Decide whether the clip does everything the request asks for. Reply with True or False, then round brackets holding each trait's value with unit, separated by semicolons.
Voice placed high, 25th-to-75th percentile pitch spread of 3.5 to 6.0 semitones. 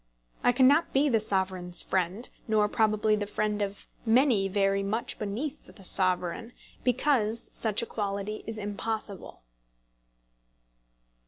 False (210 Hz; 2.8 semitones)